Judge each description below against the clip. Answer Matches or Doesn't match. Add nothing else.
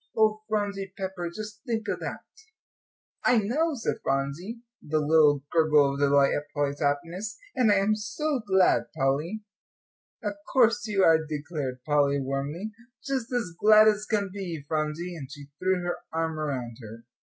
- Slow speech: Doesn't match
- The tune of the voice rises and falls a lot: Matches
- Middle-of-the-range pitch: Matches